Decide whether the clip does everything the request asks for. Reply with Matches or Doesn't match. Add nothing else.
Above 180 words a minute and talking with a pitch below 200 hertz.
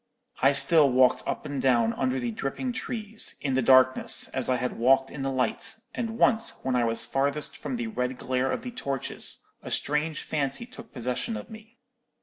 Matches